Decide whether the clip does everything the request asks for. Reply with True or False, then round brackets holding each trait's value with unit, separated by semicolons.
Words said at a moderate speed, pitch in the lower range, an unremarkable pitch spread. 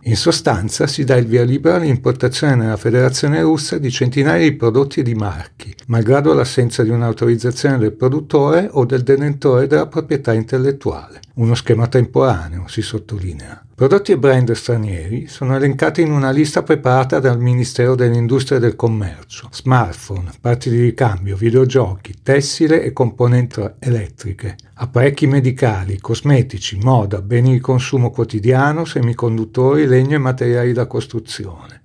True (140 wpm; 125 Hz; 3.1 semitones)